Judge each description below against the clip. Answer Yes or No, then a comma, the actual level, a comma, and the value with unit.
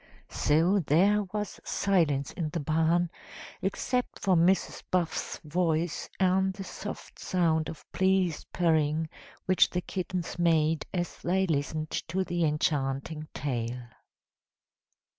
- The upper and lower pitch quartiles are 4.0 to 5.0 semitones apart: No, average, 3.2 semitones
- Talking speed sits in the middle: No, slow, 120 wpm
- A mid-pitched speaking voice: Yes, medium, 170 Hz